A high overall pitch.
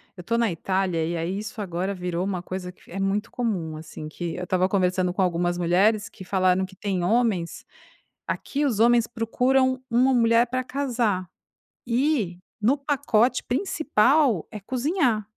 Yes: high, 205 Hz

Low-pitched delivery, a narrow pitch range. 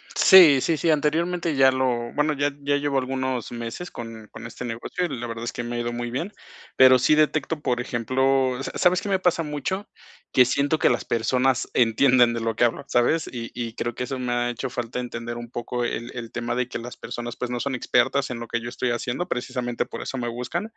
No: low, 125 Hz; average, 3.1 semitones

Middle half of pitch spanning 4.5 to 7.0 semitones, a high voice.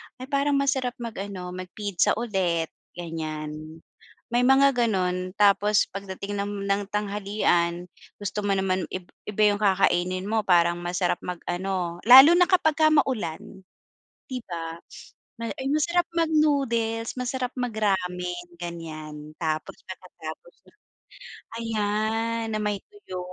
Yes: average, 5.1 semitones; high, 200 Hz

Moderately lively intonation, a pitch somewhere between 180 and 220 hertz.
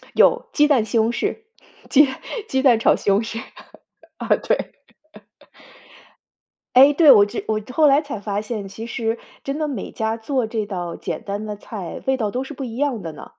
No: average, 4.4 semitones; high, 230 Hz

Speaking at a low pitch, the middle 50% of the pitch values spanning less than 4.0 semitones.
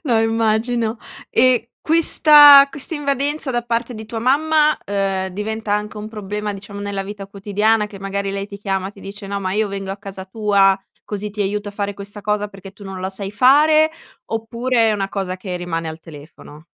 No: high, 210 Hz; average, 2.8 semitones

